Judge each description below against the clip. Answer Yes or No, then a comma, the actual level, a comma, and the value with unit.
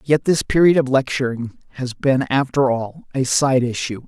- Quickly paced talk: No, average, 175 wpm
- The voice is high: No, low, 130 Hz